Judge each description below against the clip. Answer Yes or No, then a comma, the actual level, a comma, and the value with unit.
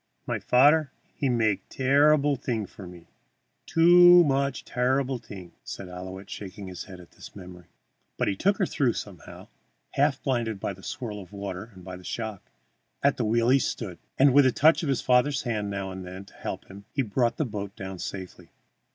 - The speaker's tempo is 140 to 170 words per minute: No, average, 195 wpm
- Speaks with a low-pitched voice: Yes, low, 115 Hz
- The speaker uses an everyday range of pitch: No, wide, 6.1 semitones